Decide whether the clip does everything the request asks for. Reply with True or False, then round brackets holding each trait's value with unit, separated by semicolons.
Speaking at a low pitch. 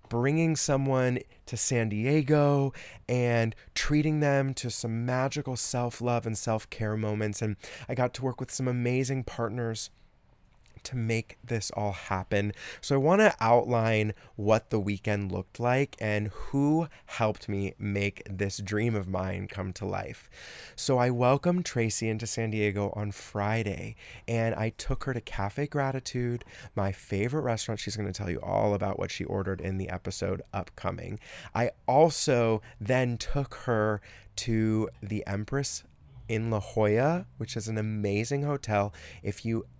True (110 Hz)